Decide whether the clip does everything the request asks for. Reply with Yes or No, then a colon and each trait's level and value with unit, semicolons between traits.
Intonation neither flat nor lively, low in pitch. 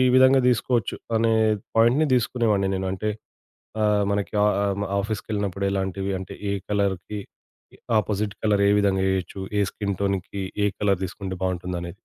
No: narrow, 1.9 semitones; low, 100 Hz